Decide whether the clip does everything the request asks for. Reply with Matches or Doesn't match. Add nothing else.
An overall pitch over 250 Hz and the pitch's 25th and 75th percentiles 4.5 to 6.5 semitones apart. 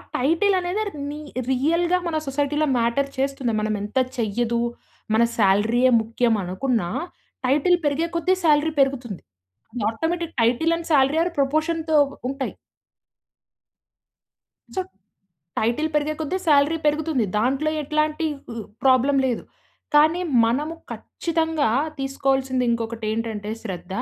Matches